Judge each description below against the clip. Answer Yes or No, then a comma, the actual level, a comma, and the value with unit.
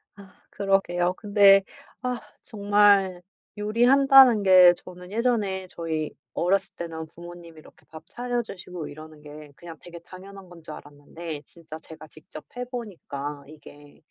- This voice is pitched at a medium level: Yes, medium, 180 Hz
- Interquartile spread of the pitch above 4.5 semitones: No, average, 4.2 semitones